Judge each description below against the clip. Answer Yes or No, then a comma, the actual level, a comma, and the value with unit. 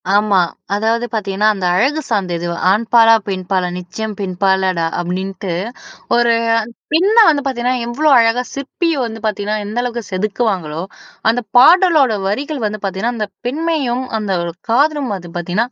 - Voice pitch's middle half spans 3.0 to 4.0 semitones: No, average, 4.7 semitones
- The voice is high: Yes, high, 220 Hz